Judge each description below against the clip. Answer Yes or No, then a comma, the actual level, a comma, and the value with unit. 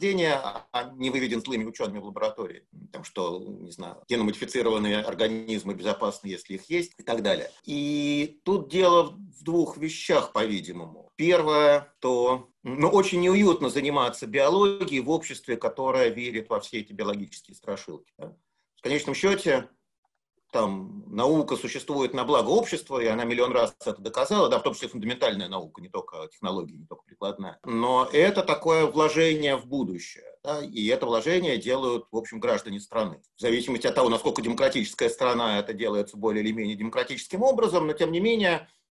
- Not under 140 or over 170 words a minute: Yes, fast, 160 wpm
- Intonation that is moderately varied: No, wide, 7.3 semitones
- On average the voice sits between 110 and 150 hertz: Yes, medium, 140 Hz